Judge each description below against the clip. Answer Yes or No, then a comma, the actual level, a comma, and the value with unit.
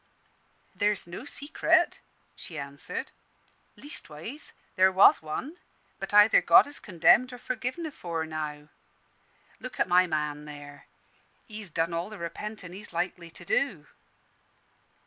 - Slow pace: Yes, slow, 125 wpm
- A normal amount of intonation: No, wide, 5.7 semitones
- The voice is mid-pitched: Yes, medium, 180 Hz